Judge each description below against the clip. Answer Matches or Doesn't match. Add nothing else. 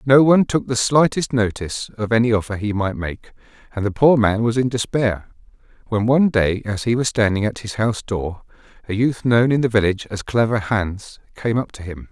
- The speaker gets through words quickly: Matches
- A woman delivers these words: Doesn't match